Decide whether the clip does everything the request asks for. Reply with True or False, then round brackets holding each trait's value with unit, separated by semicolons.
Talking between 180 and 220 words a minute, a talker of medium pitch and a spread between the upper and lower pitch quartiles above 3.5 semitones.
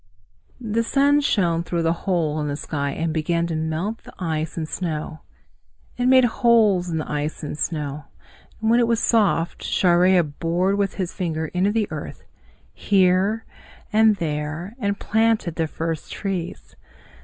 False (155 wpm; 175 Hz; 4.8 semitones)